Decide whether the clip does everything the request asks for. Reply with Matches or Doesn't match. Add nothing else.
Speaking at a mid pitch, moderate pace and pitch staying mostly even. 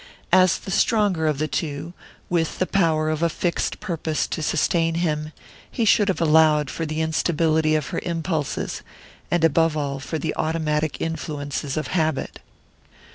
Matches